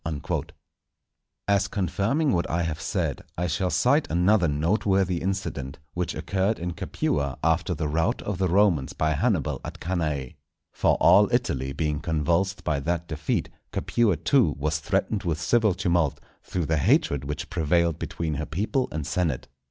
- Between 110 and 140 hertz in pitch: No, very low, 85 Hz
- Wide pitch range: No, average, 3.9 semitones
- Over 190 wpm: No, average, 160 wpm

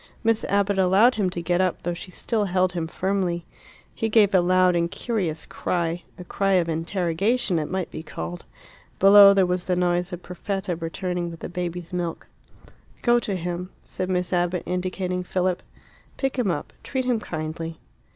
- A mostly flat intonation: Yes, narrow, 2.2 semitones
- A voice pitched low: No, medium, 180 Hz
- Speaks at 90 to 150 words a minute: No, average, 180 wpm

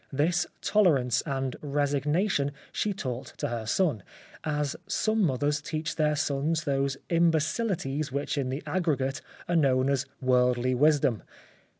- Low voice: No, medium, 145 Hz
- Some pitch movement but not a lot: Yes, average, 3.1 semitones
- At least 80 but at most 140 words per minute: Yes, slow, 135 wpm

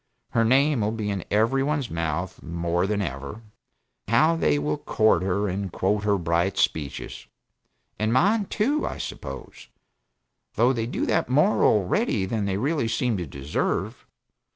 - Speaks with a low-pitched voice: Yes, low, 105 Hz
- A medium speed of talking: Yes, average, 160 wpm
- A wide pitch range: Yes, wide, 6.1 semitones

